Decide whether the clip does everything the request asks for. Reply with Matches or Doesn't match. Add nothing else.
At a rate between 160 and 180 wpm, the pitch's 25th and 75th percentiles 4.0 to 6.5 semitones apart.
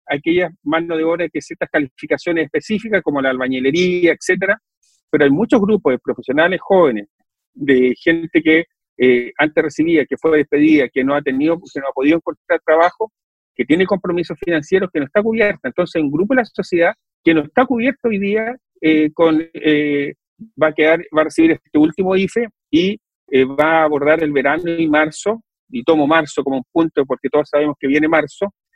Doesn't match